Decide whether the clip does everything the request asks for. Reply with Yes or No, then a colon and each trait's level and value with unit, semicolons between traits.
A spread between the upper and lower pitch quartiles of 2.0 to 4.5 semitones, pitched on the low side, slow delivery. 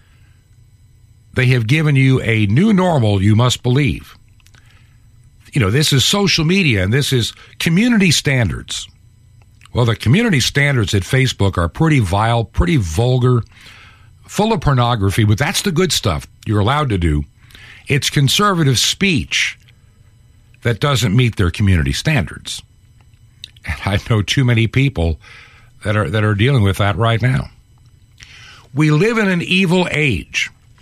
No: average, 4.0 semitones; low, 115 Hz; average, 145 wpm